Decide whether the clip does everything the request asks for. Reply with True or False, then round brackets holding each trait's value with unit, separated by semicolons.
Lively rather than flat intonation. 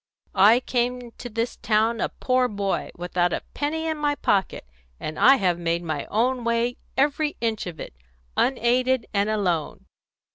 False (4.9 semitones)